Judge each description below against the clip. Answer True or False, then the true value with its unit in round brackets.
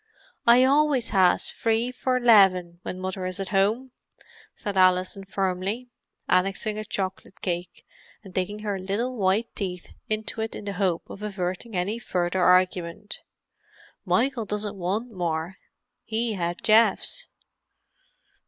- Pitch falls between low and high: False (195 Hz)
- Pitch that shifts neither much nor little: True (3.3 semitones)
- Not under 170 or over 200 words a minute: False (135 wpm)